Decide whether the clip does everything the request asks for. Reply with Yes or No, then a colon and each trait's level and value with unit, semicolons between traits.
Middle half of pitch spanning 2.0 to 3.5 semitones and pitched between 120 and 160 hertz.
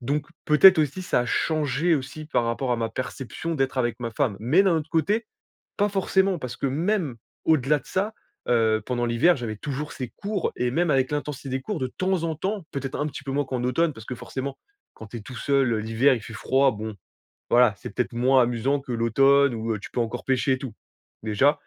No: average, 4.3 semitones; low, 135 Hz